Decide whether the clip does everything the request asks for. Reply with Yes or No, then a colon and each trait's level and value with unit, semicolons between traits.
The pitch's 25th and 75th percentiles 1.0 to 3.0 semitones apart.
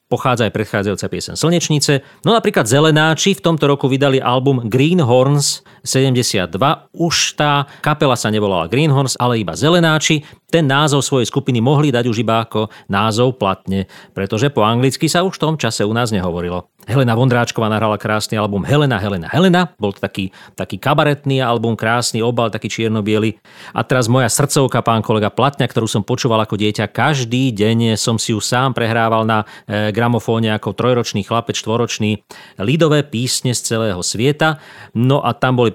No: average, 4.6 semitones